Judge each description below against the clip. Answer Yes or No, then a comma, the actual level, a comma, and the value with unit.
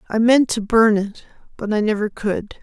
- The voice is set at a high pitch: Yes, high, 215 Hz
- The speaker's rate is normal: Yes, average, 160 wpm